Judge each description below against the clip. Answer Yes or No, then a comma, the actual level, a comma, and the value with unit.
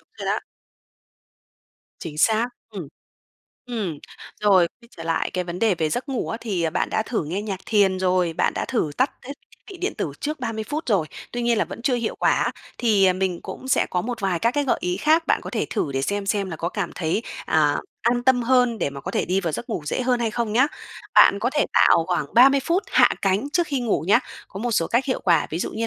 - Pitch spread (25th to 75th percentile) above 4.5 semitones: Yes, wide, 5.4 semitones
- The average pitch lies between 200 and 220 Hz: Yes, high, 215 Hz